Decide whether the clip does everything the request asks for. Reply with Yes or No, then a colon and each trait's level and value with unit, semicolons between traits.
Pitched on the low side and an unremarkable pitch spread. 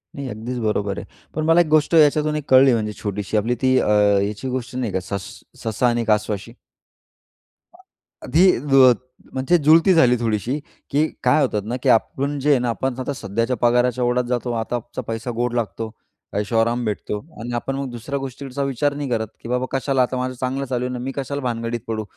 Yes: low, 125 Hz; average, 3.0 semitones